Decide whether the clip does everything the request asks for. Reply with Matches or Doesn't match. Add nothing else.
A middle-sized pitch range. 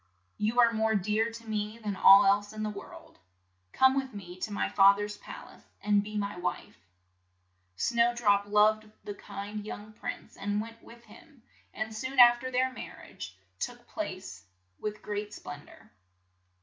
Doesn't match